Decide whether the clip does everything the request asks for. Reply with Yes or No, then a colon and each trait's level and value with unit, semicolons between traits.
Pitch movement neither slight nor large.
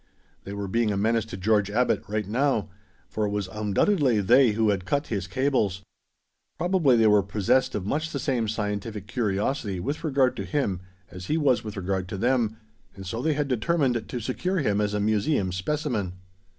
Yes: average, 4.7 semitones